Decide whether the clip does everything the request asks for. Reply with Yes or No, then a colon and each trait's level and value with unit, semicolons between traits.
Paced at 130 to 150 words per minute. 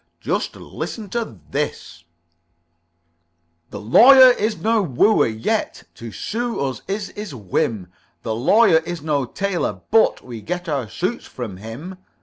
Yes: slow, 135 wpm